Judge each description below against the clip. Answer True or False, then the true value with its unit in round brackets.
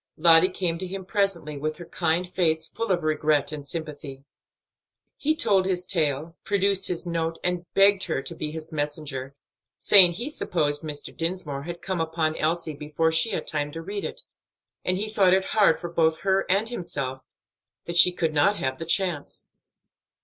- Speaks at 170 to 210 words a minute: True (180 wpm)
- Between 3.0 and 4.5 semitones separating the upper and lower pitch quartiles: True (3.4 semitones)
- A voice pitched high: False (165 Hz)